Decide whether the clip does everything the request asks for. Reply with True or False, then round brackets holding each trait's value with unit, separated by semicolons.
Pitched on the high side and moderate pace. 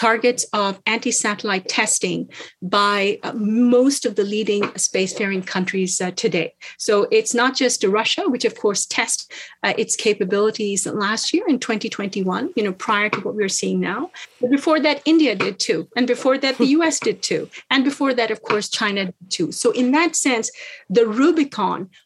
True (225 Hz; 175 wpm)